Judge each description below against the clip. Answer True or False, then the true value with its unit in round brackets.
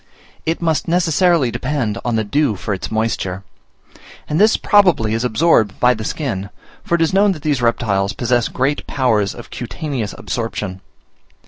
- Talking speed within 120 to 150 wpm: False (160 wpm)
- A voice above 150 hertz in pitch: False (125 Hz)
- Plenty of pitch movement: True (6.5 semitones)